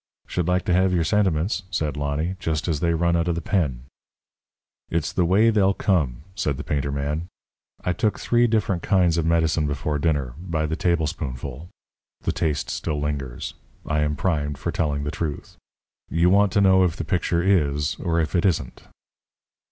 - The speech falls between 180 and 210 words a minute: Yes, average, 185 wpm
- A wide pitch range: No, average, 3.6 semitones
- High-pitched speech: No, very low, 80 Hz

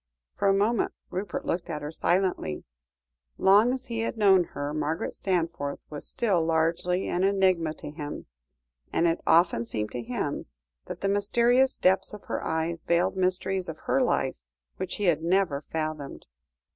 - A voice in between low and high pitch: Yes, medium, 175 Hz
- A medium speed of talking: Yes, average, 165 wpm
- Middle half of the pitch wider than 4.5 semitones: No, average, 3.9 semitones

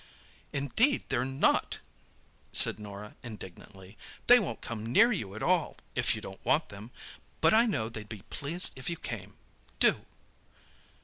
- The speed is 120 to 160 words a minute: Yes, average, 145 wpm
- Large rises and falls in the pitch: Yes, wide, 8.4 semitones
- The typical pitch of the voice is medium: No, low, 120 Hz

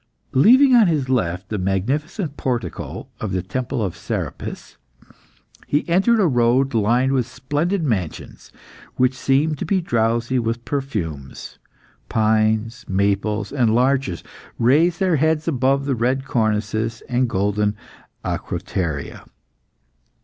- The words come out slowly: Yes, slow, 120 wpm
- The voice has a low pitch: Yes, low, 125 Hz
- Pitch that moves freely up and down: No, average, 4.8 semitones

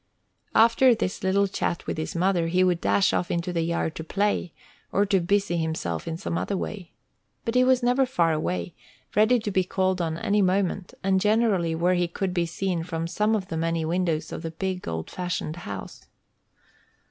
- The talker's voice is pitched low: No, medium, 180 Hz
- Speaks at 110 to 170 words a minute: No, average, 195 wpm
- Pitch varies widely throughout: No, average, 3.3 semitones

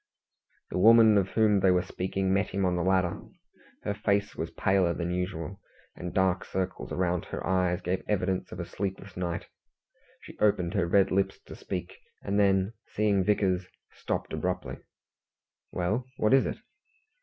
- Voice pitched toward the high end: No, very low, 95 Hz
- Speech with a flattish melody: Yes, narrow, 1.9 semitones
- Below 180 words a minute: Yes, average, 165 wpm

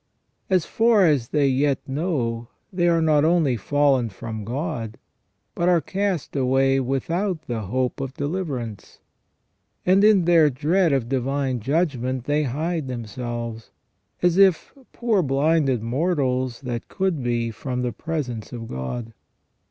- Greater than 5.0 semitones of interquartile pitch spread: Yes, wide, 5.4 semitones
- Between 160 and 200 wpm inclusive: No, slow, 135 wpm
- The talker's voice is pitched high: No, low, 135 Hz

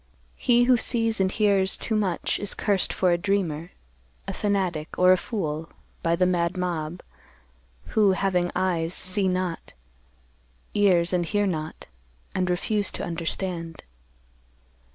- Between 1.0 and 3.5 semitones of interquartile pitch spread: Yes, average, 2.9 semitones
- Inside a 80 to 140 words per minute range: Yes, slow, 135 wpm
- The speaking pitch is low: No, medium, 185 Hz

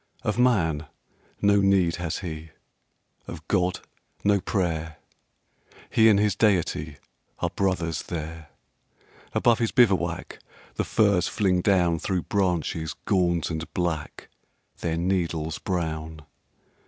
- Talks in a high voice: No, very low, 90 Hz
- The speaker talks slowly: Yes, slow, 115 wpm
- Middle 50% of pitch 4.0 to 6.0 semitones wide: No, average, 3.4 semitones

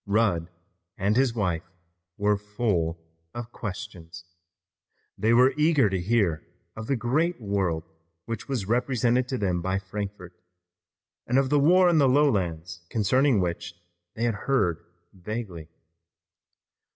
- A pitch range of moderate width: No, wide, 5.7 semitones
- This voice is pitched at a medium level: No, low, 105 Hz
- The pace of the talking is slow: Yes, slow, 130 wpm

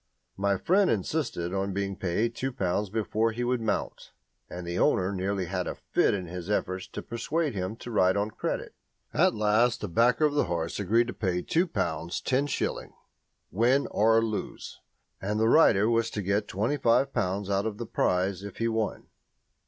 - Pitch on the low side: Yes, low, 105 Hz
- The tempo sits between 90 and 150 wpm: No, average, 185 wpm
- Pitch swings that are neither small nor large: Yes, average, 3.8 semitones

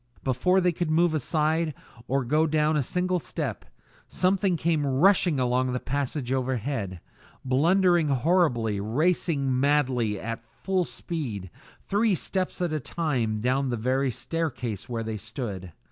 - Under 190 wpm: Yes, average, 140 wpm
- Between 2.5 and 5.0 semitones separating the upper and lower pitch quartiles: No, wide, 5.5 semitones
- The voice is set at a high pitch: No, medium, 140 Hz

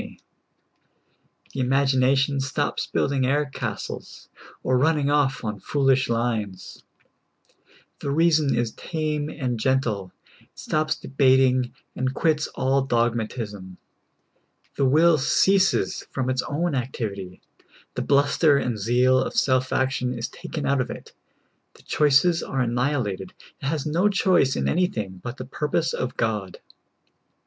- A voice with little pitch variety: No, average, 3.4 semitones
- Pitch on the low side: Yes, low, 130 Hz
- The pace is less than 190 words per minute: Yes, slow, 135 wpm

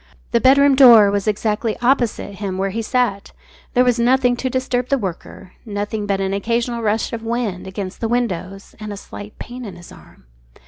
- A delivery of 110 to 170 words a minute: No, average, 190 wpm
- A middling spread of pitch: Yes, average, 3.6 semitones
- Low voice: No, high, 225 Hz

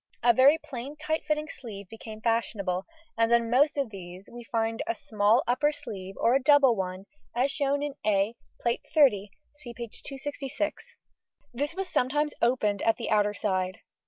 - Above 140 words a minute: Yes, average, 170 wpm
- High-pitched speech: Yes, high, 240 Hz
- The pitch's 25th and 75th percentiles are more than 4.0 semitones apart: Yes, average, 5.3 semitones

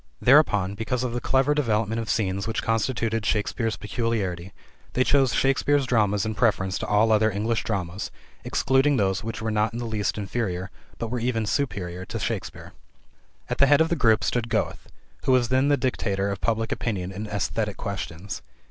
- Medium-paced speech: Yes, average, 185 wpm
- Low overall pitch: Yes, low, 110 Hz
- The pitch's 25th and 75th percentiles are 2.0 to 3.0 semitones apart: No, average, 3.4 semitones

